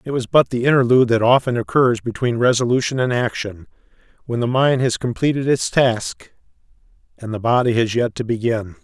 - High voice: No, low, 120 Hz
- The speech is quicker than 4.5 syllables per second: Yes, 5.5 syllables/s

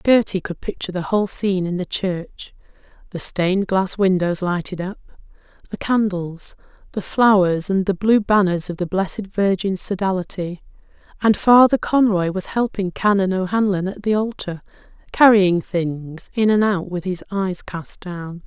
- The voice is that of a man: No, female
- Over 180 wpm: No, average, 155 wpm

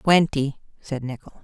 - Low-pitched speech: No, medium, 145 Hz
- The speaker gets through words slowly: Yes, slow, 125 wpm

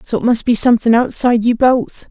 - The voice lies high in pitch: Yes, high, 235 Hz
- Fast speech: Yes, fast, 230 wpm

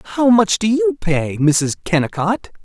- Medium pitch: Yes, medium, 180 Hz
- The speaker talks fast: No, average, 160 wpm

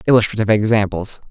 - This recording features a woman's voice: No, male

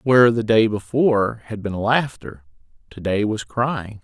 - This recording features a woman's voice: No, male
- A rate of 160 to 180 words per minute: Yes, average, 165 wpm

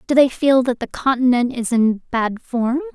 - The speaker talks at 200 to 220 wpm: Yes, fast, 205 wpm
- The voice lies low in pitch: No, very high, 250 Hz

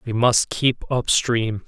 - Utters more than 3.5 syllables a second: No, 3.2 syllables/s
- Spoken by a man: Yes, male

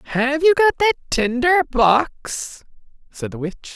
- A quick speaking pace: No, average, 145 wpm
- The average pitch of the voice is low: No, very high, 285 Hz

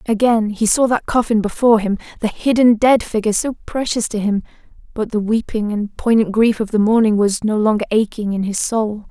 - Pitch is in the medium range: No, high, 220 Hz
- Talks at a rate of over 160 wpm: Yes, fast, 205 wpm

